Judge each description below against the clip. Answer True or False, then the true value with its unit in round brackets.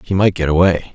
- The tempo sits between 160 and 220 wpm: False (255 wpm)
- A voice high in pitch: False (90 Hz)